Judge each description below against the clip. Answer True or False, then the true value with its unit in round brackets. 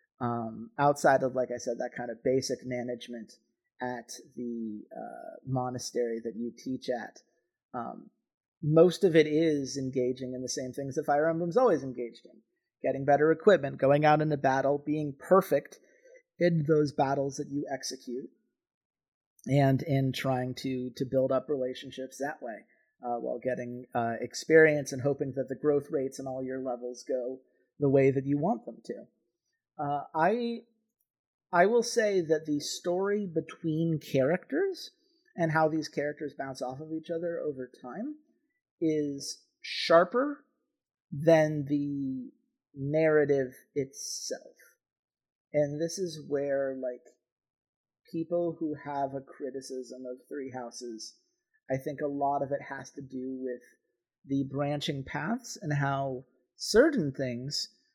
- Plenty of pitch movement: False (3.9 semitones)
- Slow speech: False (145 wpm)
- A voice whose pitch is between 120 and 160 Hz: True (140 Hz)